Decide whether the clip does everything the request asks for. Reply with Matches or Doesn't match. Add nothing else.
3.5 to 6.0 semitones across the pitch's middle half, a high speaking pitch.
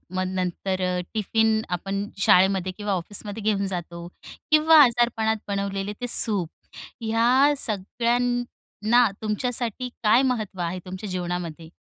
Matches